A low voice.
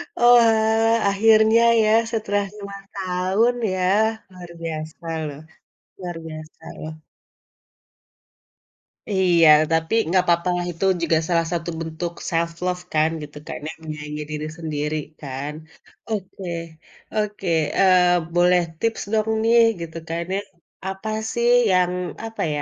No: medium, 180 Hz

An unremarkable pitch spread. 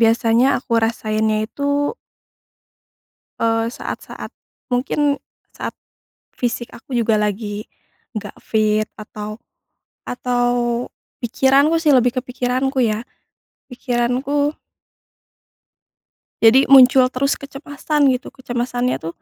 Yes: average, 3.2 semitones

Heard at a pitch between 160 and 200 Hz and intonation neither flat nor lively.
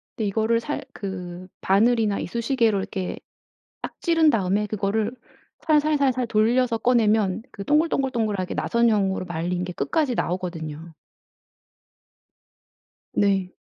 No: high, 215 Hz; average, 4.5 semitones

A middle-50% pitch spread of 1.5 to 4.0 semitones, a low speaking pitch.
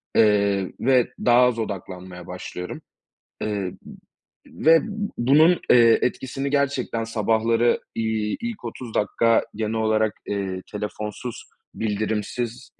Yes: average, 2.9 semitones; low, 110 Hz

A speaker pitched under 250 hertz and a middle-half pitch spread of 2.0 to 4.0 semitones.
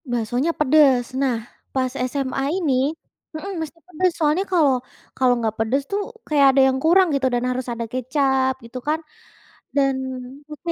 No: very high, 270 Hz; average, 3.3 semitones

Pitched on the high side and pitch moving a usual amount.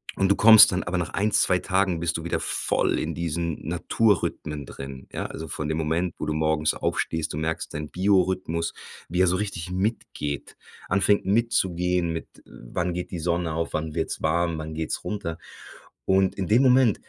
No: very low, 85 Hz; average, 3.2 semitones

